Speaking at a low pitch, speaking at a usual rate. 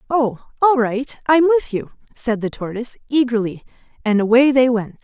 No: high, 245 Hz; average, 165 wpm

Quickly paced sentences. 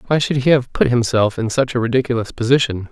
Yes: fast, 225 wpm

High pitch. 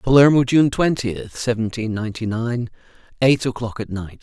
No: low, 120 Hz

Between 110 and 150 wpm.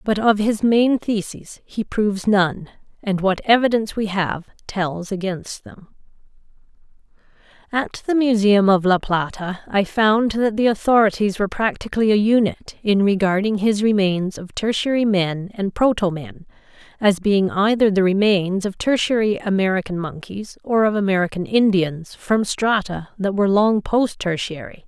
Yes: average, 145 wpm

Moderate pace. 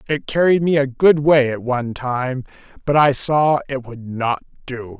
Yes: average, 190 wpm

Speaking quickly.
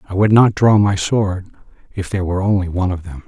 Yes: fast, 240 wpm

